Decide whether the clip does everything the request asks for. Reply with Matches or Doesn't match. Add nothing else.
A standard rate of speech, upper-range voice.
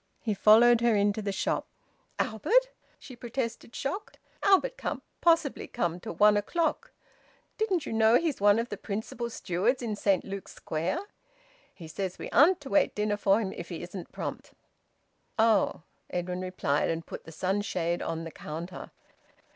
Matches